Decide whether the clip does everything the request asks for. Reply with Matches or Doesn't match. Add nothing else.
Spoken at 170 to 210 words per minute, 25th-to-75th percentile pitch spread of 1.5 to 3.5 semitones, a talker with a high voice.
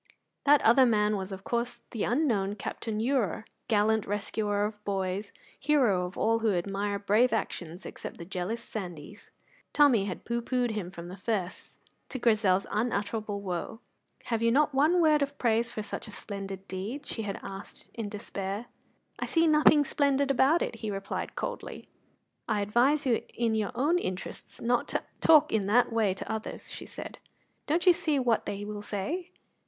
Doesn't match